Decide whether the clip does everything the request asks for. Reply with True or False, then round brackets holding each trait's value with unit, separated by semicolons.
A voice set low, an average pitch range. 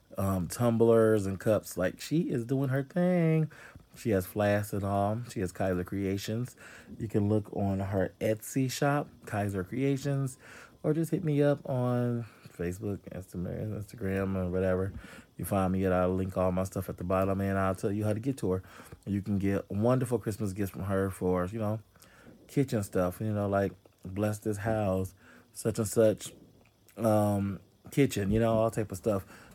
True (105 Hz; 3.4 semitones)